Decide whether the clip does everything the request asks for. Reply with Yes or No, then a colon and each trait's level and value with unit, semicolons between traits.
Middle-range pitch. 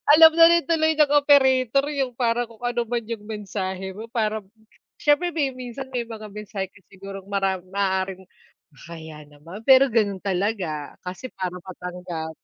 No: high, 210 Hz